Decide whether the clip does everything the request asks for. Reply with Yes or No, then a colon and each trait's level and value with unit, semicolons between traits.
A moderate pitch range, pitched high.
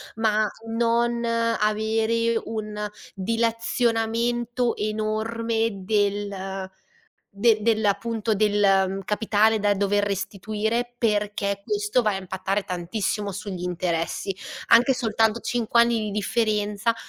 No: narrow, 2.2 semitones; high, 215 Hz